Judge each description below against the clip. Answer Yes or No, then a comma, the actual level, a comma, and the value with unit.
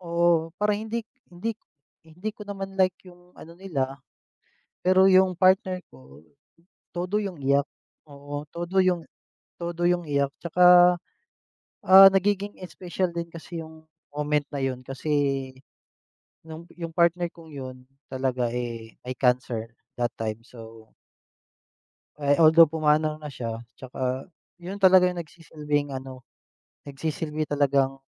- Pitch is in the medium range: Yes, medium, 160 Hz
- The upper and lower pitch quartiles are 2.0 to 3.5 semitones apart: No, average, 4.8 semitones